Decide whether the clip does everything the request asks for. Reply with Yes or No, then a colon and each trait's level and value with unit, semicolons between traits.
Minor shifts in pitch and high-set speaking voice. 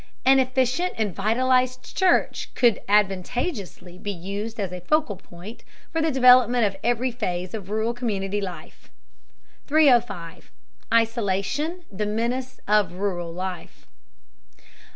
No: average, 4.7 semitones; high, 220 Hz